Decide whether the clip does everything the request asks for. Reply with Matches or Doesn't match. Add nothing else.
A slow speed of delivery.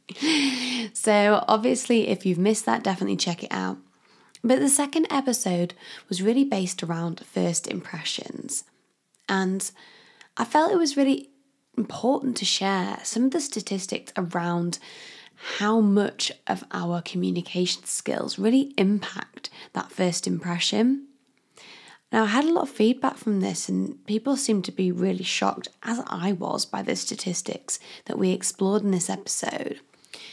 Doesn't match